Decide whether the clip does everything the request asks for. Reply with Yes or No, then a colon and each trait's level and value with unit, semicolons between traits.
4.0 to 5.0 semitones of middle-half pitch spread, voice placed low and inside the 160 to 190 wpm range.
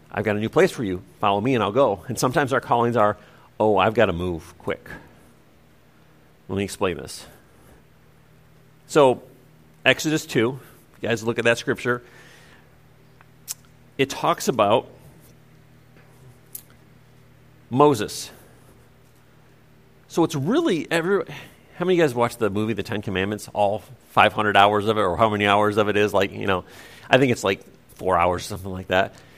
Yes: average, 4.3 semitones; low, 120 Hz; average, 165 wpm